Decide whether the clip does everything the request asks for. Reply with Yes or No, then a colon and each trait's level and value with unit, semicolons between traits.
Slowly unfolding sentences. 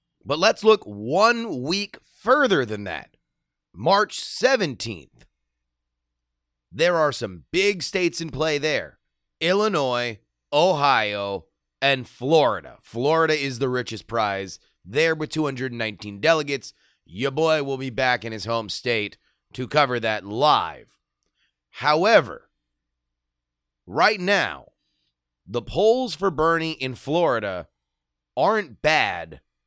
Yes: slow, 110 wpm